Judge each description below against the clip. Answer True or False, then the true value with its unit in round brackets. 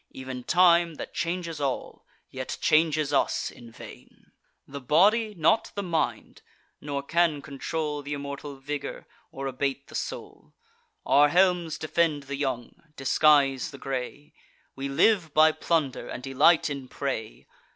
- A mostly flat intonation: False (3.3 semitones)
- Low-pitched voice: False (145 Hz)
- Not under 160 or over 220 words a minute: False (140 wpm)